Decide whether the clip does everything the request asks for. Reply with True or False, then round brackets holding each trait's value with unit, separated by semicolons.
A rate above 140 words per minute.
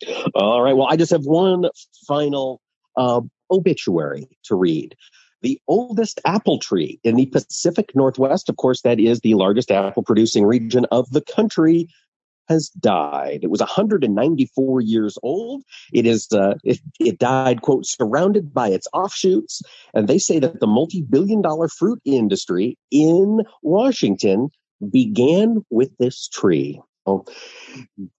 False (135 wpm)